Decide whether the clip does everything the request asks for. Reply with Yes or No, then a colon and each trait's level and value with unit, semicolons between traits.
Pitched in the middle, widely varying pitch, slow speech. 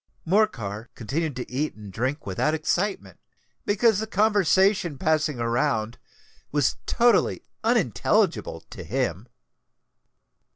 Yes: medium, 150 Hz; wide, 9.0 semitones; slow, 100 wpm